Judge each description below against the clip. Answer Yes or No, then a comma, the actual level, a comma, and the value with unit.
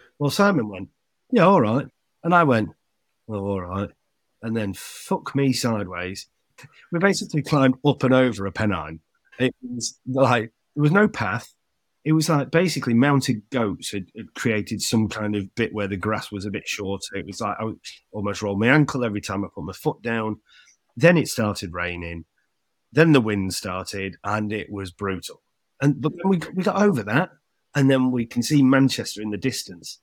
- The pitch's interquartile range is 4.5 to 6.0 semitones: Yes, wide, 5.4 semitones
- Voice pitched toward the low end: Yes, low, 115 Hz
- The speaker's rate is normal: Yes, average, 190 wpm